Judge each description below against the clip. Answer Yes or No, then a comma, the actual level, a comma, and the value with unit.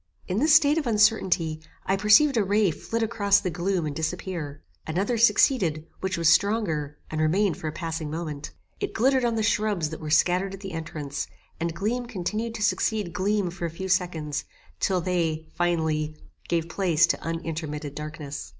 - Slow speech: No, average, 175 wpm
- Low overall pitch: No, medium, 180 Hz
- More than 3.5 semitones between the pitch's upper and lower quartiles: Yes, average, 4.9 semitones